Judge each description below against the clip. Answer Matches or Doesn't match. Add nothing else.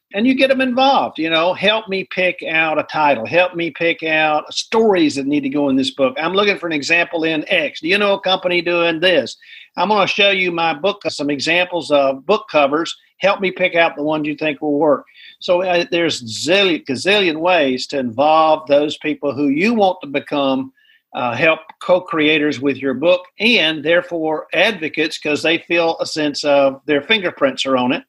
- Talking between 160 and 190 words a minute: Doesn't match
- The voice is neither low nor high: Matches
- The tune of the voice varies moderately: Matches